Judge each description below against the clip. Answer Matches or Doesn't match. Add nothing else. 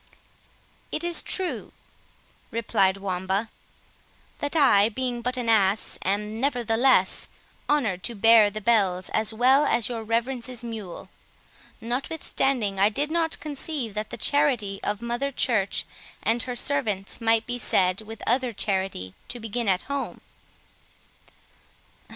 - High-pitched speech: Matches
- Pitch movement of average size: Matches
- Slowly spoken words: Matches